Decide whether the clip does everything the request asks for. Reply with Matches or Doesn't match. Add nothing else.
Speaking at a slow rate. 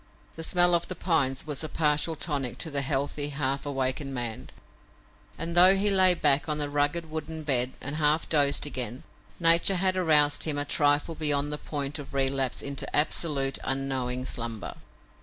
Doesn't match